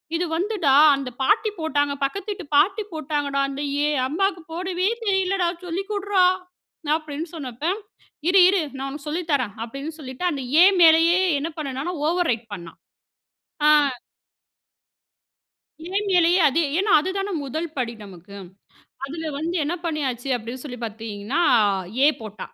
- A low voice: No, very high, 310 Hz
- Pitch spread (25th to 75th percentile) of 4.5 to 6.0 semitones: Yes, average, 5.1 semitones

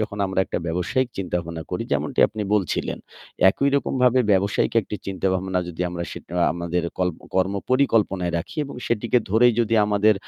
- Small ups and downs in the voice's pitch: No, average, 4.4 semitones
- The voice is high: No, very low, 95 Hz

